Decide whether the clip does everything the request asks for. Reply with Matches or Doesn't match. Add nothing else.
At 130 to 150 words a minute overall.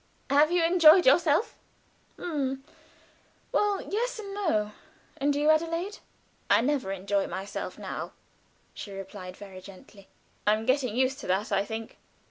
Matches